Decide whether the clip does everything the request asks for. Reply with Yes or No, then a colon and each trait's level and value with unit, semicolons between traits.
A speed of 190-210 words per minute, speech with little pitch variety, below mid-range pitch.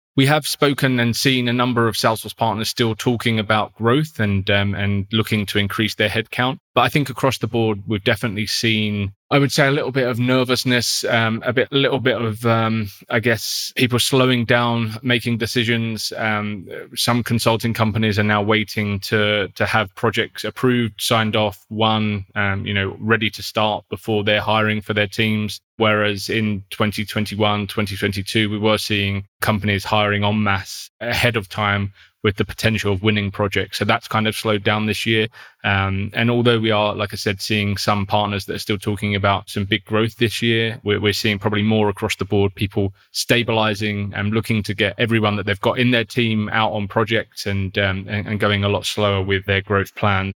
Yes: average, 200 wpm; narrow, 2.0 semitones; low, 110 Hz